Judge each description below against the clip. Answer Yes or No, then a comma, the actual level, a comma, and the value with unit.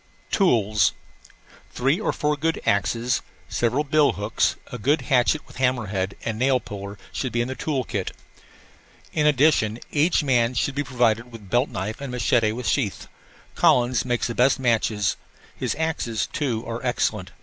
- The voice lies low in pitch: Yes, low, 120 Hz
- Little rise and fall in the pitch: No, average, 4.0 semitones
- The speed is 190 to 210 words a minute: No, average, 170 wpm